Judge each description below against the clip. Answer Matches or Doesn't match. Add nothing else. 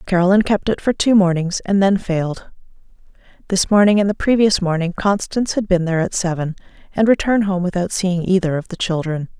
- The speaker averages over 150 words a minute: Matches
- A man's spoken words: Doesn't match